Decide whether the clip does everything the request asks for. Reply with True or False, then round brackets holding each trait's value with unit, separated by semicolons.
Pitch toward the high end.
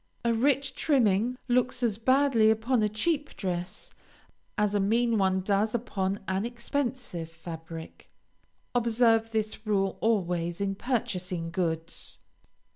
True (215 Hz)